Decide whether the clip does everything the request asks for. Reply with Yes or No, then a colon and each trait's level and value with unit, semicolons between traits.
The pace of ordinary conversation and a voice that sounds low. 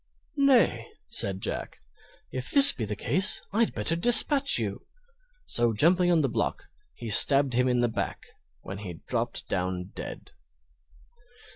Yes: average, 145 wpm; low, 125 Hz